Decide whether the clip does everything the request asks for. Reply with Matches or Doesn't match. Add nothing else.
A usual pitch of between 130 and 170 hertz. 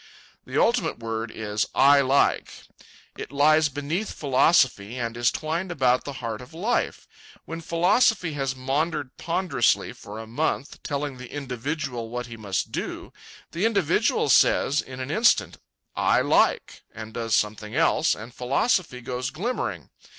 Matches